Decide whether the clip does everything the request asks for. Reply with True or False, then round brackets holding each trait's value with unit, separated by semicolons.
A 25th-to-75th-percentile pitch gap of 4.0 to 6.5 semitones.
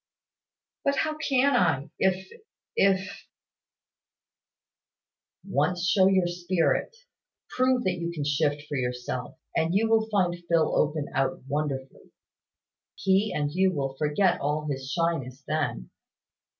True (4.7 semitones)